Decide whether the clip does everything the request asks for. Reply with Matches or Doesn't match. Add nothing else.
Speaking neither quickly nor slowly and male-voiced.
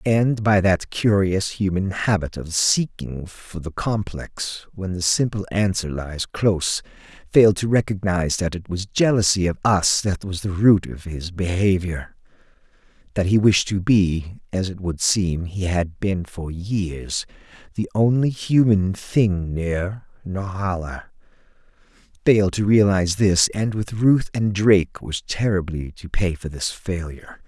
Matches